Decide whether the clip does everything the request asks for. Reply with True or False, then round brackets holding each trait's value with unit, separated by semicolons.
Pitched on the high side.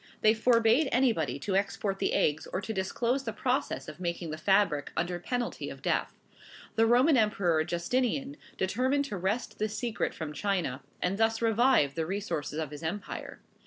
True (205 Hz)